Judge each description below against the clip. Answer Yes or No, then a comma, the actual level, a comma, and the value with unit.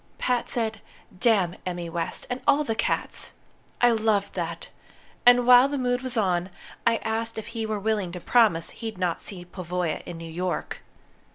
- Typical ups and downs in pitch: Yes, average, 4.8 semitones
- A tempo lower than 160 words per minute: No, average, 175 wpm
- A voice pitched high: Yes, high, 215 Hz